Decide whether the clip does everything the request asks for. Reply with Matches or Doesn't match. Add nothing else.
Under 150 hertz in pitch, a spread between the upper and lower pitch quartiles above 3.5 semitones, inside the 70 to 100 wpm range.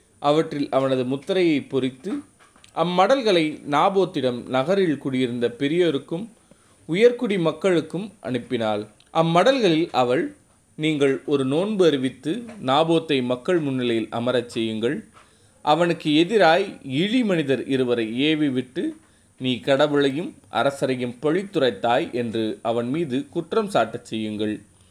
Matches